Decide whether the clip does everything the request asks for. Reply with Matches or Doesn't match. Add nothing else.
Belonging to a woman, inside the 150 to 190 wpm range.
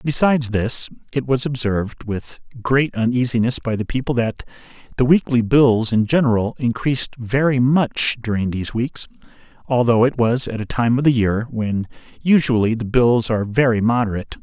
Doesn't match